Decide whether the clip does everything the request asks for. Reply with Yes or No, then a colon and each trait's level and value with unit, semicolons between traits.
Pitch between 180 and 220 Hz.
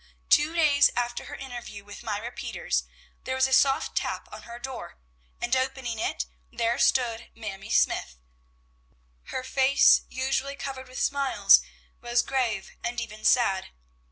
No: high, 245 Hz